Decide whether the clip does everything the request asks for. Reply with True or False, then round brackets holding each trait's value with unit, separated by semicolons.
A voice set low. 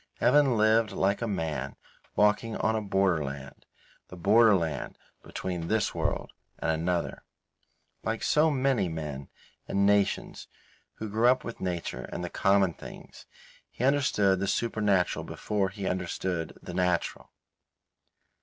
True (100 Hz)